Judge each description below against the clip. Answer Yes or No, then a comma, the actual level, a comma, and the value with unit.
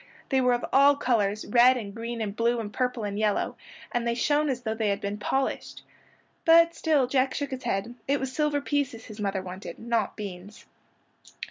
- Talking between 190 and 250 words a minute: Yes, average, 200 wpm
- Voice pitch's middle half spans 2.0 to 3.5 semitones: No, average, 4.3 semitones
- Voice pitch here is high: Yes, high, 235 Hz